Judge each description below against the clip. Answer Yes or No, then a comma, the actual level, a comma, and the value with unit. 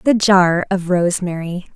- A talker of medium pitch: Yes, medium, 180 Hz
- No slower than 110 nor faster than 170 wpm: Yes, slow, 135 wpm